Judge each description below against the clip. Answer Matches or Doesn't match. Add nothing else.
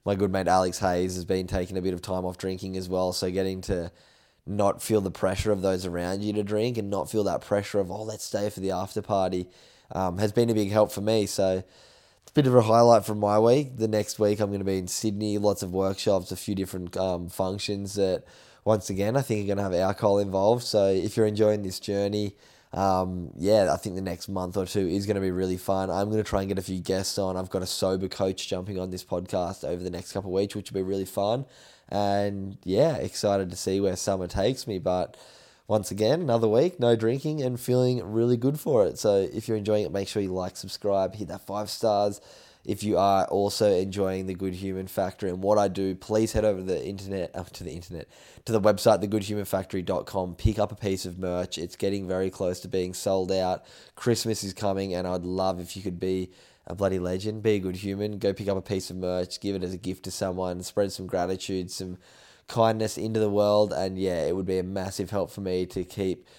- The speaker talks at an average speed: Doesn't match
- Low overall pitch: Matches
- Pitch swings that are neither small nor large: Doesn't match